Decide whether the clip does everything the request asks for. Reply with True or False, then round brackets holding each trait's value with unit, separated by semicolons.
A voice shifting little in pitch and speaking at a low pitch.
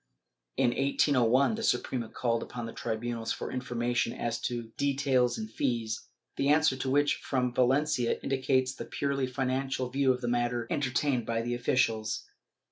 True (2.2 semitones; 125 Hz)